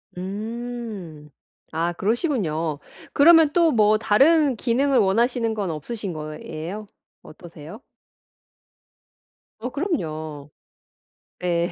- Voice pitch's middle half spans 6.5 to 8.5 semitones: Yes, wide, 6.9 semitones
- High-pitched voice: Yes, high, 210 Hz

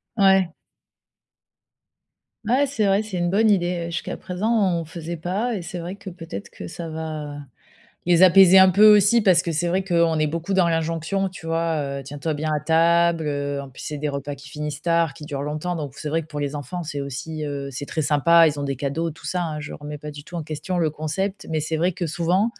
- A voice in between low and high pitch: Yes, medium, 165 Hz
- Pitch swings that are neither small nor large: Yes, average, 3.4 semitones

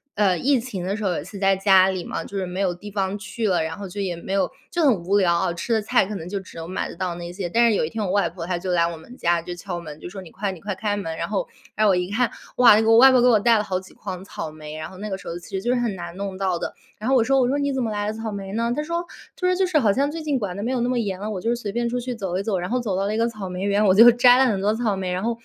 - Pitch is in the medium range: No, high, 200 Hz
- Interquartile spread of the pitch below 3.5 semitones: No, average, 4.2 semitones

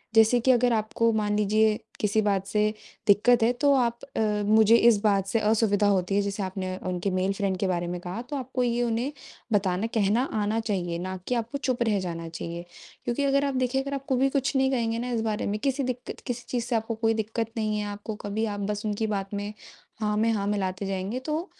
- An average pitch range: Yes, average, 3.1 semitones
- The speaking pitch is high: Yes, high, 220 Hz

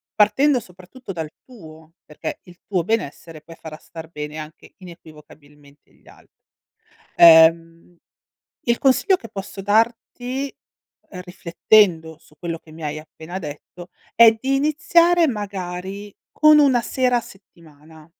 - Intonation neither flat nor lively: No, wide, 6.5 semitones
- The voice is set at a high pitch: No, medium, 180 Hz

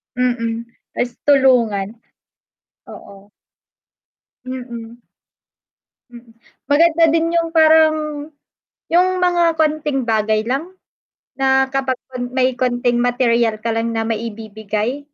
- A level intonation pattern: No, average, 4.3 semitones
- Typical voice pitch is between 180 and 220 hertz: No, high, 245 Hz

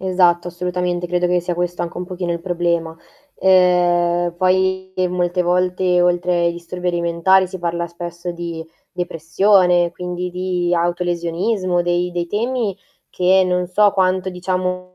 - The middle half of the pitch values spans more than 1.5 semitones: No, narrow, 0.9 semitones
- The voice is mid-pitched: Yes, medium, 180 Hz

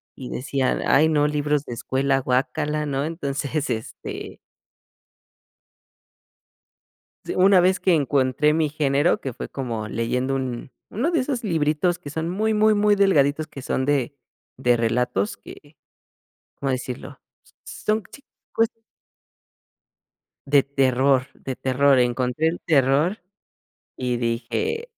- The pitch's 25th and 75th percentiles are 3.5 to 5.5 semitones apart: Yes, average, 3.8 semitones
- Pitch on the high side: No, medium, 140 Hz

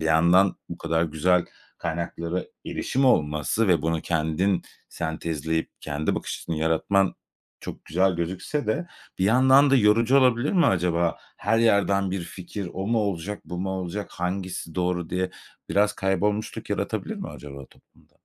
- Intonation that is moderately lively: Yes, average, 3.9 semitones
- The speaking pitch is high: No, very low, 90 Hz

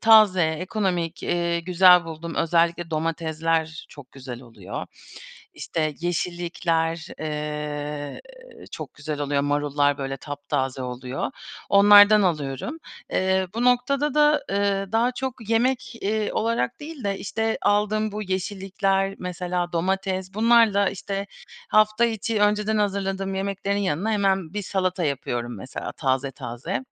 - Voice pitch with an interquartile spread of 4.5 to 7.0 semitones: Yes, average, 5.0 semitones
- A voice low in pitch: No, medium, 185 Hz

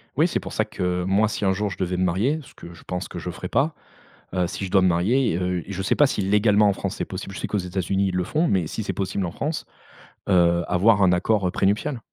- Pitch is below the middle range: Yes, very low, 95 Hz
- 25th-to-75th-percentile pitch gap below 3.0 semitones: Yes, narrow, 2.6 semitones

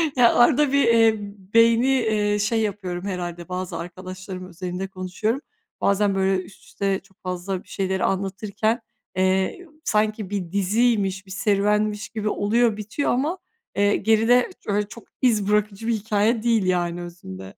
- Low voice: No, high, 205 Hz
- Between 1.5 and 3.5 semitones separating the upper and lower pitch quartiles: Yes, average, 3.1 semitones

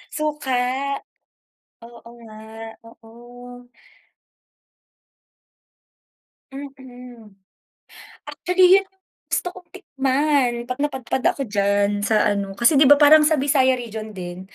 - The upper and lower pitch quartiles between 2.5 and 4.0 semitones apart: No, average, 4.7 semitones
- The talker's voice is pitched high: Yes, very high, 250 Hz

